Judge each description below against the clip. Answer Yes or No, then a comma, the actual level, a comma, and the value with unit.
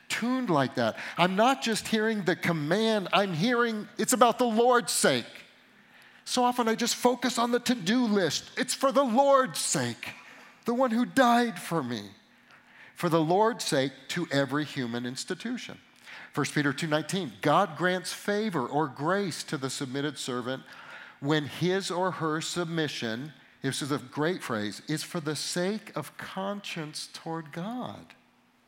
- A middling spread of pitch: No, wide, 7.5 semitones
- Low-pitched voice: No, medium, 180 Hz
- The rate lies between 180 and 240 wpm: No, average, 155 wpm